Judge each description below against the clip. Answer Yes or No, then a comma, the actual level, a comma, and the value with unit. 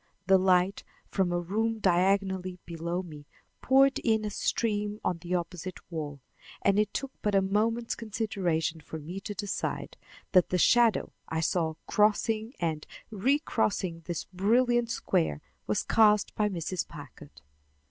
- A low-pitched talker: No, high, 190 Hz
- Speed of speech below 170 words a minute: Yes, average, 145 wpm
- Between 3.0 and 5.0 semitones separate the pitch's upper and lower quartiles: Yes, average, 4.0 semitones